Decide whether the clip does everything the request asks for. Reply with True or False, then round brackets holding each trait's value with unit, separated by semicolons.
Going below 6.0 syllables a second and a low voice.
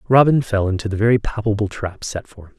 False (6.1 syllables/s; 110 Hz)